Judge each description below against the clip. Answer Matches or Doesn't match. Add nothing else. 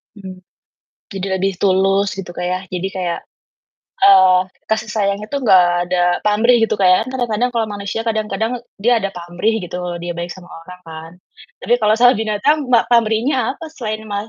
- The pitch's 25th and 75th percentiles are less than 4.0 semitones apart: Matches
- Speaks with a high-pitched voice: Matches